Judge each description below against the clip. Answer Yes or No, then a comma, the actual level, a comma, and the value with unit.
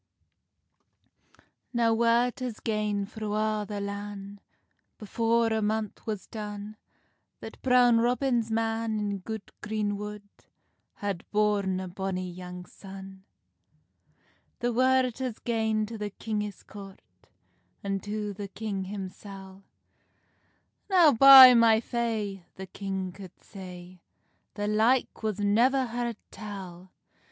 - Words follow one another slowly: Yes, slow, 120 wpm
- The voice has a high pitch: Yes, high, 210 Hz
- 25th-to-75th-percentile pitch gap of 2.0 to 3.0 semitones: Yes, narrow, 2.5 semitones